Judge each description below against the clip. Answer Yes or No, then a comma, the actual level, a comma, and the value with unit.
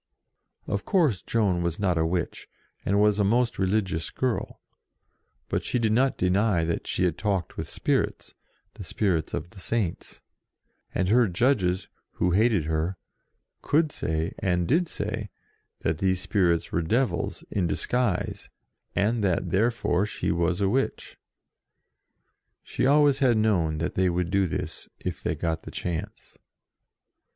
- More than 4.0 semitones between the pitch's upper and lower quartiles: Yes, average, 4.6 semitones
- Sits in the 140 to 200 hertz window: No, very low, 95 Hz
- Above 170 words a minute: No, average, 150 wpm